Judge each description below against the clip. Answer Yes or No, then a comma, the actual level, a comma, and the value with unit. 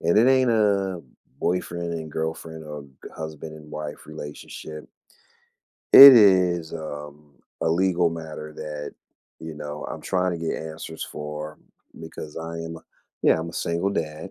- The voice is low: Yes, very low, 80 Hz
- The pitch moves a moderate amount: No, narrow, 2.3 semitones